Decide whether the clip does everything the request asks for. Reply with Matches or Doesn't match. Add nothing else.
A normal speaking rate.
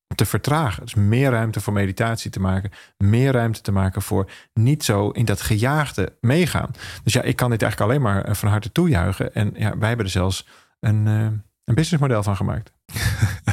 Matches